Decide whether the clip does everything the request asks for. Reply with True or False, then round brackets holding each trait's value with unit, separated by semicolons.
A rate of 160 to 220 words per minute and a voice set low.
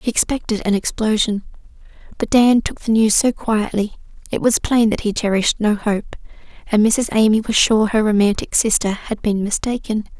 False (175 wpm; 215 Hz)